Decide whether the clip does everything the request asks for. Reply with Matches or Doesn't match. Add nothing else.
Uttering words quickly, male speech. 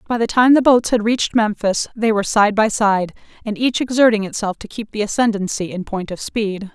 Doesn't match